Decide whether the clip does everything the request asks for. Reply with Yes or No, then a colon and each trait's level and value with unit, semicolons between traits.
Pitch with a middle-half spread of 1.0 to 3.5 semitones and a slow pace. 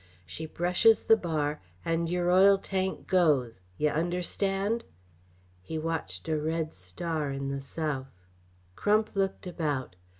No: average, 4.4 semitones; slow, 130 wpm